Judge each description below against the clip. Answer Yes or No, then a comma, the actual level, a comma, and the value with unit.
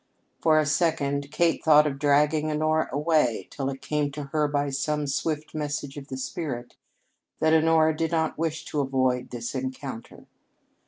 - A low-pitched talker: No, medium, 150 Hz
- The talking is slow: No, average, 165 wpm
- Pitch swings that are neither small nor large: No, narrow, 2.3 semitones